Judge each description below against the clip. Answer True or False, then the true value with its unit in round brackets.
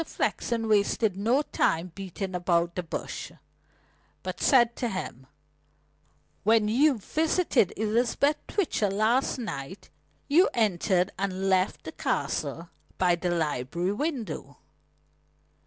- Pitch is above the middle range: True (200 Hz)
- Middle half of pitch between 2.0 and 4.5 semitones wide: False (5.1 semitones)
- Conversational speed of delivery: False (110 wpm)